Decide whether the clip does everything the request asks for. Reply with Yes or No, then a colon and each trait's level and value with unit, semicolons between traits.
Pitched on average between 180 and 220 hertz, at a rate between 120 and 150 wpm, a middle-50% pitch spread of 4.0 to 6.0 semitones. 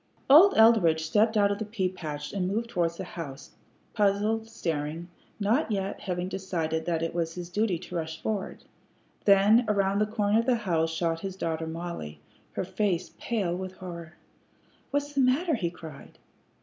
No: medium, 185 Hz; average, 175 wpm; average, 4.3 semitones